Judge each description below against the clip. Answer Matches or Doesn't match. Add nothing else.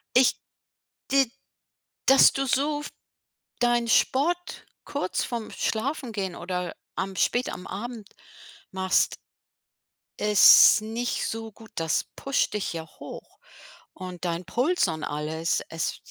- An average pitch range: Doesn't match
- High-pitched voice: Matches